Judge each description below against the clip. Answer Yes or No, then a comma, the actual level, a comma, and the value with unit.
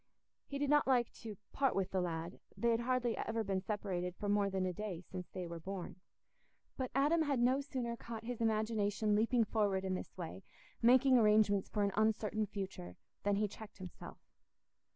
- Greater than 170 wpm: Yes, average, 180 wpm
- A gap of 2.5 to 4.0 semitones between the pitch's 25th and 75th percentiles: Yes, average, 3.6 semitones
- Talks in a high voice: Yes, high, 210 Hz